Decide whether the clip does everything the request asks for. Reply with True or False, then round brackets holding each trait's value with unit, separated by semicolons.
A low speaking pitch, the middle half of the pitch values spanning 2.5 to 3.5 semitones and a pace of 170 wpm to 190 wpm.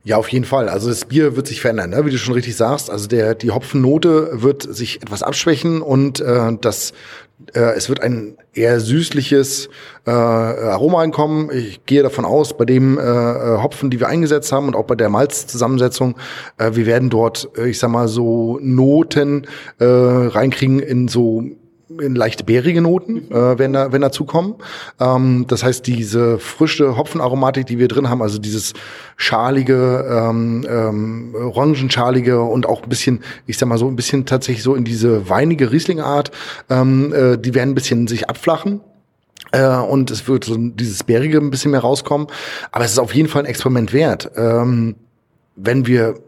True (125 Hz; 3.2 semitones; 180 wpm)